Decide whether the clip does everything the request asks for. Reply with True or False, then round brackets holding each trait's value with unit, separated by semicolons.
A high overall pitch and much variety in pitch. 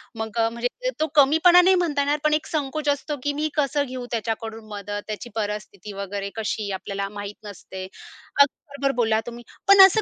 True (240 Hz; 6.1 semitones)